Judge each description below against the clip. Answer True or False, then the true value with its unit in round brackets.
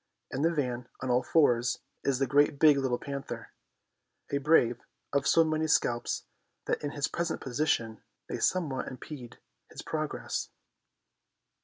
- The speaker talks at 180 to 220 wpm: False (140 wpm)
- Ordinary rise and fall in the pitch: True (3.6 semitones)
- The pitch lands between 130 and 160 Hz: True (140 Hz)